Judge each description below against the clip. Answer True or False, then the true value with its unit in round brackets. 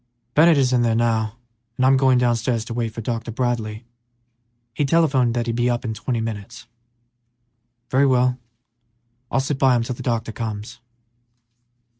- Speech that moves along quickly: False (165 wpm)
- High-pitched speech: False (120 Hz)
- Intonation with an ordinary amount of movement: False (2.2 semitones)